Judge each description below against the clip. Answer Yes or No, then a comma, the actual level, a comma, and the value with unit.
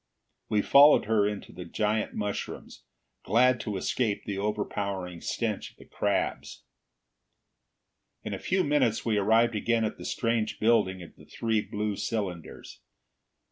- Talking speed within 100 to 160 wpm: Yes, average, 140 wpm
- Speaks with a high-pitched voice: No, low, 105 Hz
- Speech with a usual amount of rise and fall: No, narrow, 2.3 semitones